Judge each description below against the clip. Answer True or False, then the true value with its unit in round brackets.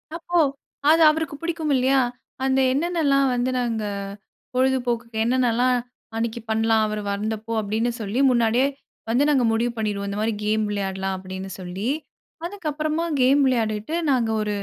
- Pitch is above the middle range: True (240 Hz)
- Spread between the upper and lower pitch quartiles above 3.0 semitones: True (4.0 semitones)